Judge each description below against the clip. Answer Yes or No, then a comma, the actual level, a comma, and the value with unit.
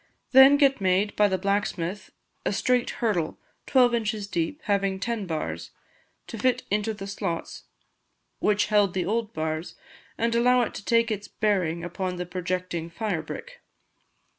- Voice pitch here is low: No, high, 205 Hz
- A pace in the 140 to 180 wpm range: Yes, average, 155 wpm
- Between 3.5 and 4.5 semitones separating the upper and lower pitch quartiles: Yes, average, 4.2 semitones